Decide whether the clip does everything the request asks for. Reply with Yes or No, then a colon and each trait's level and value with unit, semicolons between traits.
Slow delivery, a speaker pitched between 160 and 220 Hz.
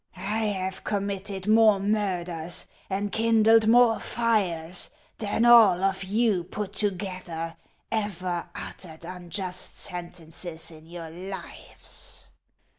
Yes: slow, 110 wpm; high, 190 Hz